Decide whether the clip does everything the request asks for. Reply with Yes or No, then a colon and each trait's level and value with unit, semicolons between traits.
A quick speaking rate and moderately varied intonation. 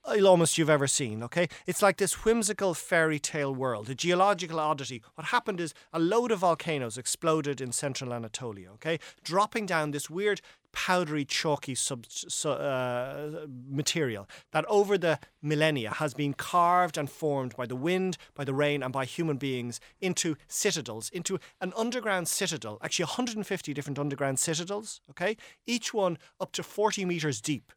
No: average, 160 wpm; average, 5.0 semitones